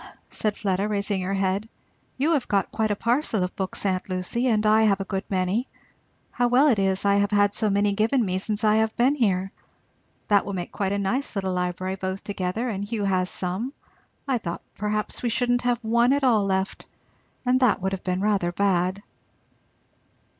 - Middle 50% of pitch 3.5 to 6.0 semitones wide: No, average, 3.1 semitones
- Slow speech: No, average, 200 wpm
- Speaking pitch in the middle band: No, high, 205 Hz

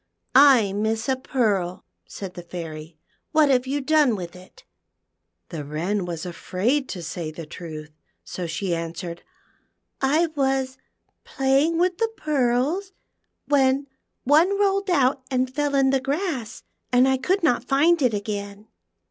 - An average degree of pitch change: No, wide, 7.7 semitones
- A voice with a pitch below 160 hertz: No, very high, 255 Hz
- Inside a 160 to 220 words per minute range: No, average, 150 wpm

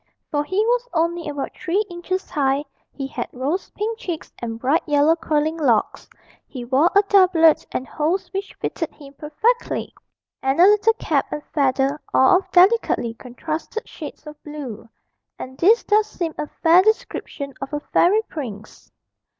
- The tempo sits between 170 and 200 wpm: No, average, 160 wpm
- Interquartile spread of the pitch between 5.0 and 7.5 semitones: Yes, average, 5.3 semitones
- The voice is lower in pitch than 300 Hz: No, very high, 315 Hz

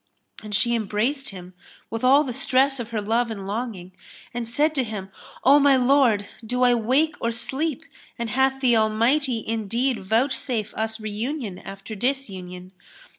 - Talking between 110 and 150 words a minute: No, average, 165 wpm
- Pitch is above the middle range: Yes, high, 235 Hz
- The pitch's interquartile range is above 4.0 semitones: No, average, 3.7 semitones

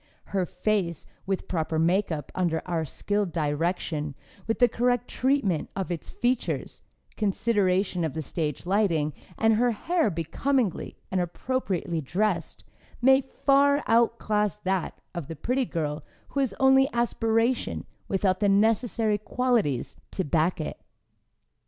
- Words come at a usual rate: No, slow, 130 wpm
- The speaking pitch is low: No, high, 195 Hz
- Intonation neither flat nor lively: No, wide, 5.9 semitones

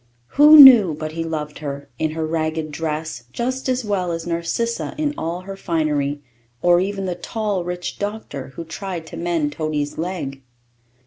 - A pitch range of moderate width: Yes, average, 4.0 semitones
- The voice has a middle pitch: Yes, medium, 170 Hz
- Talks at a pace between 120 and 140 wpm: No, average, 170 wpm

